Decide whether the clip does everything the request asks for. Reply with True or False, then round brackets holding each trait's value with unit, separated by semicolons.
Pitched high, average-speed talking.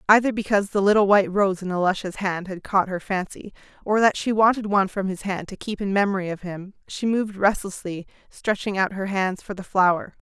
False (195 Hz; 215 wpm)